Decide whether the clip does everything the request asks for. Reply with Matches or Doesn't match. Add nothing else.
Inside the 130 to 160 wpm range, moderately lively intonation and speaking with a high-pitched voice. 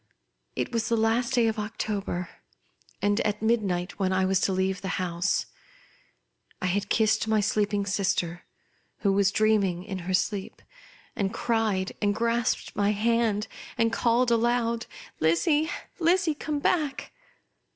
Matches